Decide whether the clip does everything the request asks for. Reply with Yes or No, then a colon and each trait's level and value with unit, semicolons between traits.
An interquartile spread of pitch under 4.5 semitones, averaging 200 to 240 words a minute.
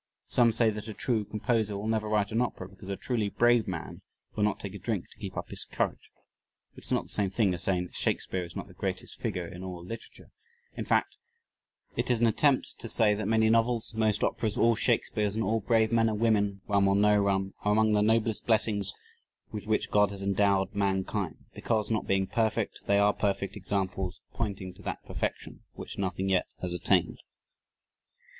Yes: narrow, 2.4 semitones; fast, 205 wpm